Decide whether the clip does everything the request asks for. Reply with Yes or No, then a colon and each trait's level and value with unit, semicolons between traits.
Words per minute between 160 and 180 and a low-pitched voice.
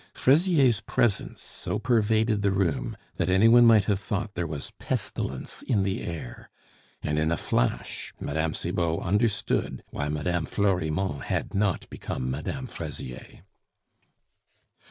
No: slow, 135 wpm; very low, 95 Hz